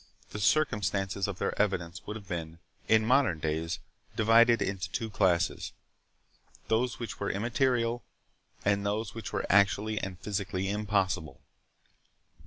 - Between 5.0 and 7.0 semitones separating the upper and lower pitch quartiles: No, average, 3.2 semitones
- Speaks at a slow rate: Yes, slow, 125 wpm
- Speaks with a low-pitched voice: Yes, low, 100 Hz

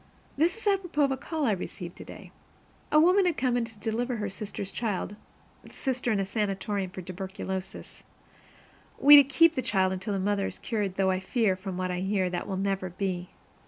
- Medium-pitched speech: No, high, 205 Hz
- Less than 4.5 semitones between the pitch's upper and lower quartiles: No, average, 5.3 semitones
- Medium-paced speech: Yes, average, 195 wpm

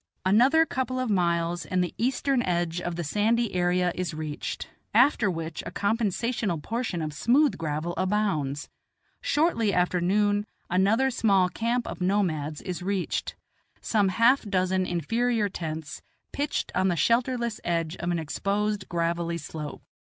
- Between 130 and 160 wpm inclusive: Yes, average, 150 wpm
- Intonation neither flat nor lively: Yes, average, 5.0 semitones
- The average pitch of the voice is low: No, medium, 185 Hz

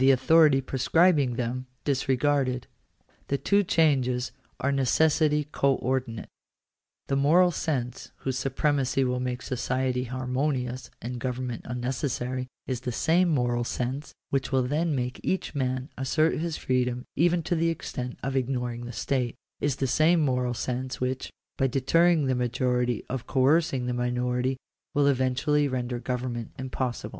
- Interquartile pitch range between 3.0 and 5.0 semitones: No, narrow, 2.6 semitones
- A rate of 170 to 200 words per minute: No, average, 145 wpm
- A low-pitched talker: Yes, low, 130 Hz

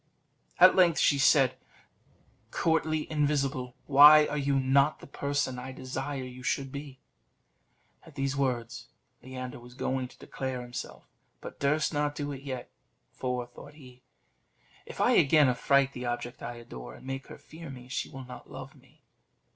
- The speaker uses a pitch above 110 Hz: Yes, low, 135 Hz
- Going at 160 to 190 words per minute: Yes, average, 165 wpm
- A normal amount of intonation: No, narrow, 2.2 semitones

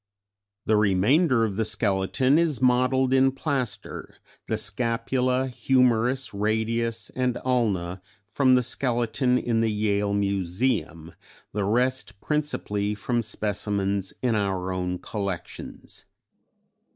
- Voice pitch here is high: No, low, 115 Hz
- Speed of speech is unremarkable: No, slow, 115 wpm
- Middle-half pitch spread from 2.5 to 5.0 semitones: Yes, average, 4.0 semitones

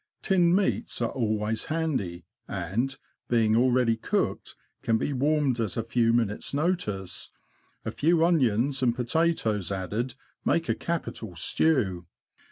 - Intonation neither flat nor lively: No, wide, 6.0 semitones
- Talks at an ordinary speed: No, slow, 130 wpm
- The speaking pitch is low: Yes, low, 120 Hz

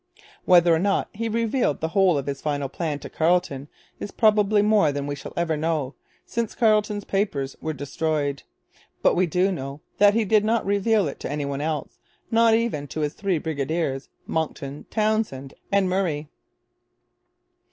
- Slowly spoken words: No, average, 170 wpm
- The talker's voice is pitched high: No, medium, 170 Hz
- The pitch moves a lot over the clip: Yes, wide, 6.2 semitones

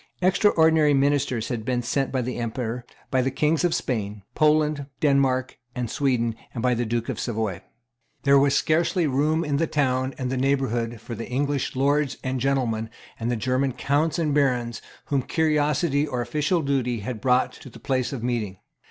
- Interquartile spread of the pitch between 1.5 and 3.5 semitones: Yes, average, 3.1 semitones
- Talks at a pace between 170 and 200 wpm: Yes, average, 180 wpm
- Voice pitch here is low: Yes, low, 130 Hz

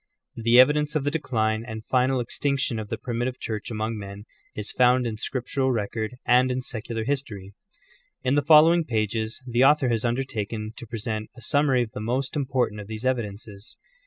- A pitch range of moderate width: Yes, average, 3.2 semitones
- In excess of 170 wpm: Yes, average, 180 wpm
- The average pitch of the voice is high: No, low, 120 Hz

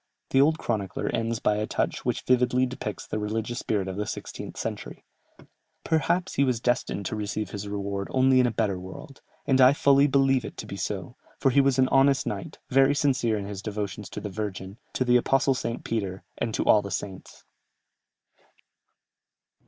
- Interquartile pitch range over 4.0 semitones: Yes, average, 4.5 semitones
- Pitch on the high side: No, low, 115 Hz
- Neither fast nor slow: Yes, average, 190 wpm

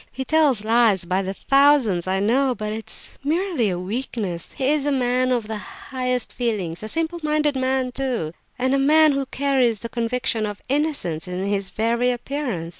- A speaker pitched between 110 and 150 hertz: No, high, 245 Hz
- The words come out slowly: No, average, 190 wpm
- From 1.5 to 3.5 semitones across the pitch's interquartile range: No, average, 4.8 semitones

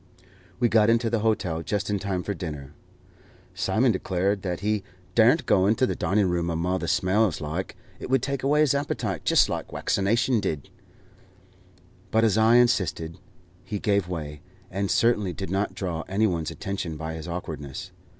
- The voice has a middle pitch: No, low, 100 Hz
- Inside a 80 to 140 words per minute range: No, average, 170 wpm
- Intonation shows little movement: No, average, 4.5 semitones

